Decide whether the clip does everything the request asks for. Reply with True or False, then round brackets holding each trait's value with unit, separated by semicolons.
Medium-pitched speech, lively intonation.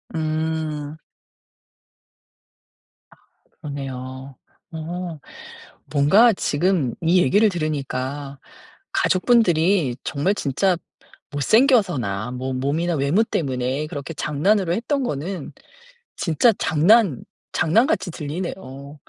False (155 Hz; 5.0 semitones)